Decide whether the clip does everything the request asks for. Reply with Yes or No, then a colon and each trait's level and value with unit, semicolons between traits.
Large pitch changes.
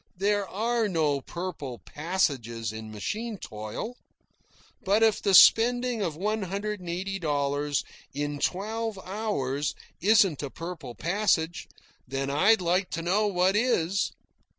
Yes: wide, 6.2 semitones